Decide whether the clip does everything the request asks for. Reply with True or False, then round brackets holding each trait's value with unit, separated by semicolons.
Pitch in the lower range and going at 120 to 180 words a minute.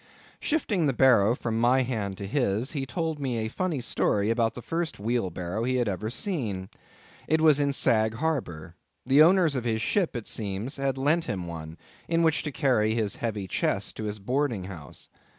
False (120 Hz; 190 wpm)